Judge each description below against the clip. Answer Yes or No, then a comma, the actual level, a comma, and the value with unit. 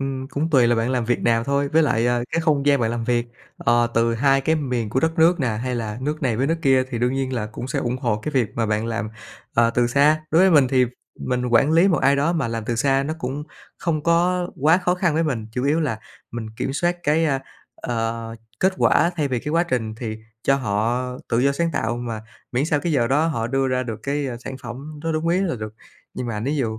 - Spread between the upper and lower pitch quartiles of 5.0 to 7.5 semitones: No, average, 4.5 semitones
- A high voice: No, low, 130 Hz